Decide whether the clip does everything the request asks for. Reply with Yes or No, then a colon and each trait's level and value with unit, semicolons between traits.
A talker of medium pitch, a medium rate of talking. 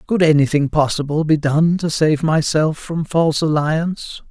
Yes: medium, 155 Hz; average, 155 wpm